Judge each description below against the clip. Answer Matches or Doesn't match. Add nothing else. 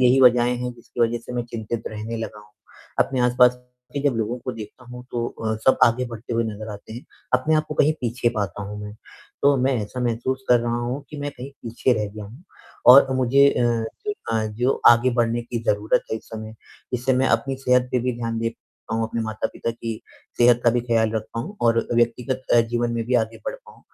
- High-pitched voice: Doesn't match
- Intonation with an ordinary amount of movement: Doesn't match